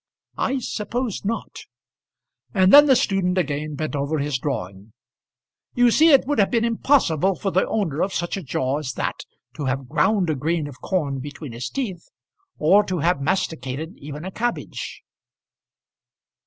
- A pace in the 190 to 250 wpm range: No, average, 165 wpm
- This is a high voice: No, medium, 170 Hz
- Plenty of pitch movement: Yes, wide, 6.5 semitones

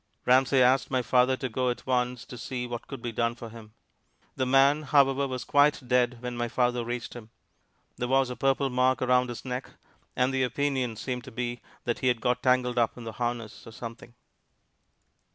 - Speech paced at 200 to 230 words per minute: Yes, fast, 205 wpm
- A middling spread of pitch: No, narrow, 1.5 semitones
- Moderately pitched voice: No, low, 125 Hz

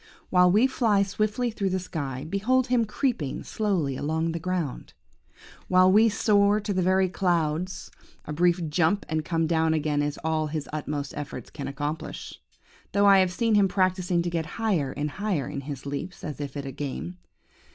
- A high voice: No, medium, 175 Hz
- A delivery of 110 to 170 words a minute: No, average, 185 wpm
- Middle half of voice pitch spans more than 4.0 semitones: Yes, average, 5.0 semitones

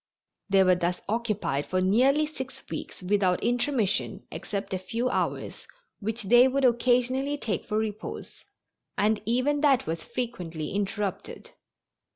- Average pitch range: Yes, average, 4.8 semitones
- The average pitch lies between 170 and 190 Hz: No, high, 220 Hz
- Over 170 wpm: No, slow, 135 wpm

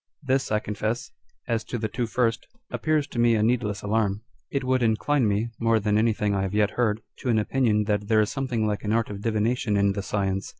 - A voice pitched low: Yes, low, 110 Hz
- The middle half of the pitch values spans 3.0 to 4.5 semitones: No, narrow, 2.4 semitones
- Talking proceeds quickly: Yes, fast, 225 wpm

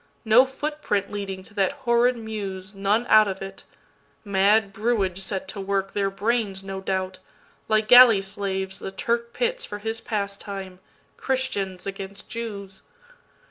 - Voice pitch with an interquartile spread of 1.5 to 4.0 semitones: Yes, average, 2.8 semitones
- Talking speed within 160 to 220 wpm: No, slow, 135 wpm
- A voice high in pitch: Yes, high, 200 Hz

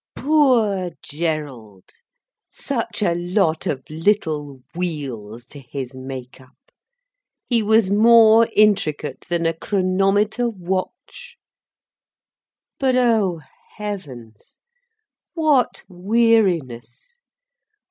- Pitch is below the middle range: No, medium, 180 Hz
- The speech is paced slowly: Yes, slow, 85 wpm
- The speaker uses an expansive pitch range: Yes, wide, 7.4 semitones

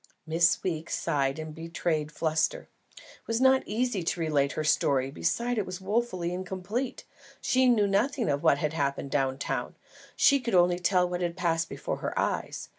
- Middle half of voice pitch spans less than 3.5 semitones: No, average, 5.2 semitones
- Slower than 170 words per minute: No, average, 180 wpm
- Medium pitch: Yes, medium, 175 Hz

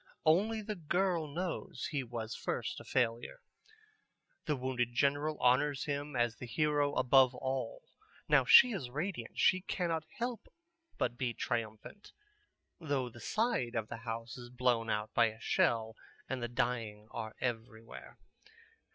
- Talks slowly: No, average, 145 wpm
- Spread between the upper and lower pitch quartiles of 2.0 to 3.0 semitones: No, average, 4.7 semitones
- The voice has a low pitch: Yes, low, 125 Hz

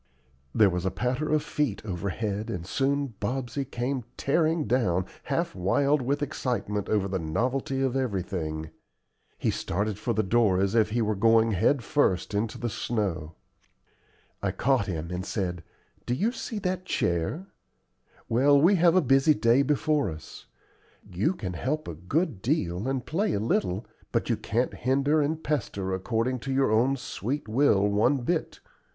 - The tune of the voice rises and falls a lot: Yes, wide, 6.2 semitones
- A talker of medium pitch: No, low, 120 Hz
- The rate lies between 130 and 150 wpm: No, average, 165 wpm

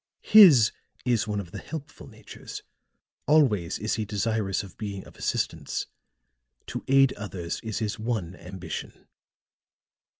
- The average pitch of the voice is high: No, low, 110 Hz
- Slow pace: Yes, slow, 130 wpm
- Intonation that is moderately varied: Yes, average, 4.1 semitones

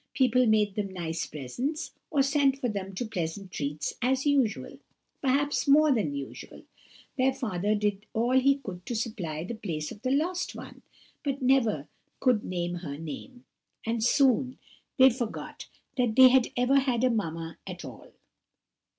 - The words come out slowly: No, average, 160 wpm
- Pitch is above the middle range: Yes, high, 230 Hz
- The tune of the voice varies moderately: No, wide, 6.2 semitones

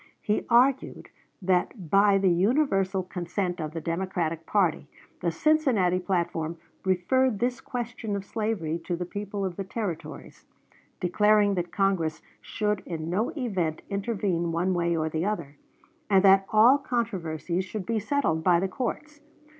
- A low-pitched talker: No, high, 190 Hz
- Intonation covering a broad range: No, average, 3.8 semitones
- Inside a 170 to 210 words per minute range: No, average, 145 wpm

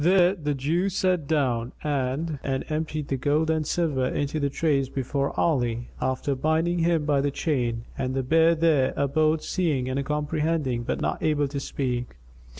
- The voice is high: No, medium, 145 Hz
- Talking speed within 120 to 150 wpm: No, average, 165 wpm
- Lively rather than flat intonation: No, average, 3.3 semitones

